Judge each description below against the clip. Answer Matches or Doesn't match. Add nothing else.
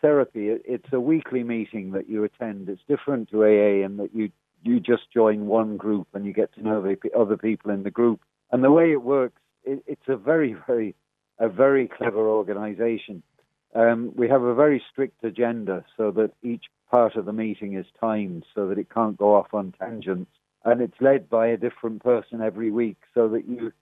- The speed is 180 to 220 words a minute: Matches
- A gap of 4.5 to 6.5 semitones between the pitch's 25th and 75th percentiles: Doesn't match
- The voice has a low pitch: Matches